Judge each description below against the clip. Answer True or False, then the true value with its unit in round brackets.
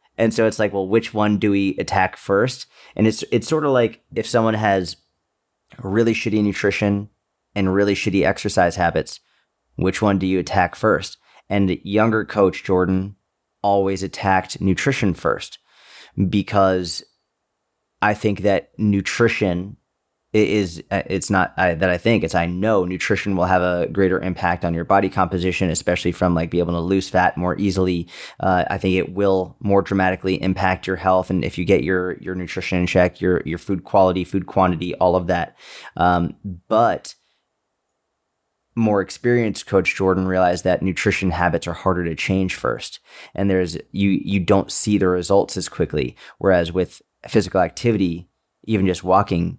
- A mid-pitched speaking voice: False (95 Hz)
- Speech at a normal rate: True (165 wpm)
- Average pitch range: False (2.0 semitones)